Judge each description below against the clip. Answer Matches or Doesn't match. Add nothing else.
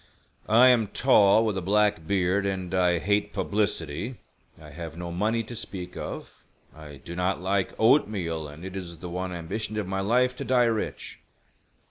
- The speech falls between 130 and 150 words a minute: Doesn't match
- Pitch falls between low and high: Doesn't match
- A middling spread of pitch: Matches